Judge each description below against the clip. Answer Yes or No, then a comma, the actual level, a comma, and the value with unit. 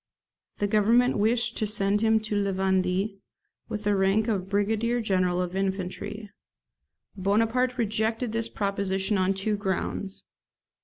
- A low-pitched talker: No, high, 205 Hz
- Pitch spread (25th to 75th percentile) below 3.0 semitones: Yes, narrow, 2.4 semitones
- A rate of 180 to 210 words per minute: No, slow, 135 wpm